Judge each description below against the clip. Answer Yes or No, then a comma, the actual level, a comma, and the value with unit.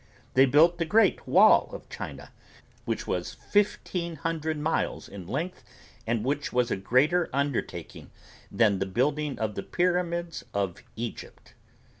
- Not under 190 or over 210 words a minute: No, average, 140 wpm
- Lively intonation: Yes, wide, 6.5 semitones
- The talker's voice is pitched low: No, medium, 145 Hz